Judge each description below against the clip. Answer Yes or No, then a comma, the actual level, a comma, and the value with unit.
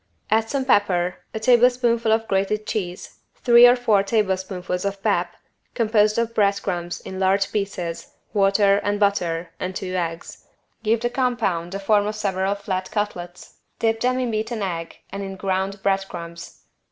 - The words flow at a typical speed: Yes, average, 165 wpm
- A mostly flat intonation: No, average, 3.0 semitones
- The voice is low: No, high, 200 Hz